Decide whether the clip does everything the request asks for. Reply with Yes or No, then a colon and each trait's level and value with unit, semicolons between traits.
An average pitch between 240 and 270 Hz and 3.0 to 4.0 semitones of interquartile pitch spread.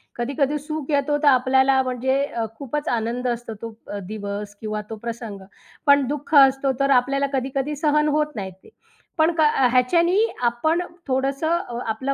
Yes: very high, 265 Hz; average, 3.6 semitones